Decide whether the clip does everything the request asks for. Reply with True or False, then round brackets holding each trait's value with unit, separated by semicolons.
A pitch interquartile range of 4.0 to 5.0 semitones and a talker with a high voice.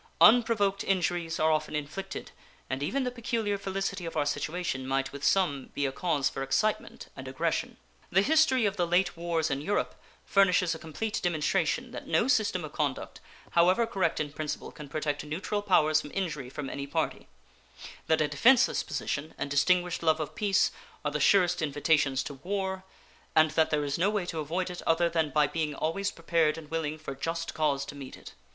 False (4.5 semitones; 165 Hz)